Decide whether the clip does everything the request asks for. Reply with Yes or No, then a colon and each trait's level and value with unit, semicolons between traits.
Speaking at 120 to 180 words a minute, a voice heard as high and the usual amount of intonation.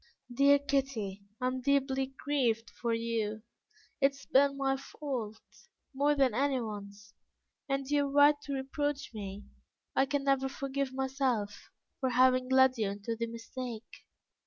Yes: average, 145 wpm; very high, 265 Hz; average, 3.3 semitones